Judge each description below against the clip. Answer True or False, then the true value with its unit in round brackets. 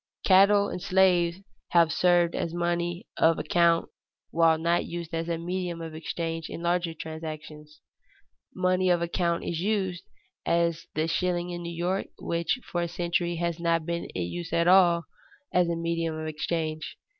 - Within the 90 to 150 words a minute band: False (165 wpm)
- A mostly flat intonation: True (1.2 semitones)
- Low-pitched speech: False (170 Hz)